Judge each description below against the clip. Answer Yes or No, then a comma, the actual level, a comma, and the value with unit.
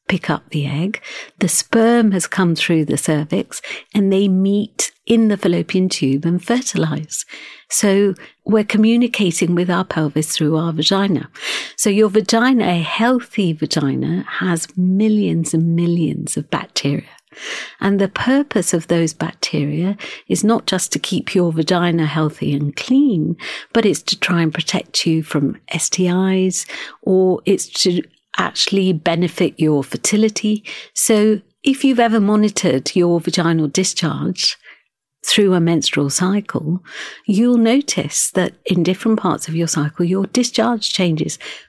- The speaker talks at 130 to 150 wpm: Yes, average, 140 wpm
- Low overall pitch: No, medium, 185 Hz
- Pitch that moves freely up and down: No, average, 4.3 semitones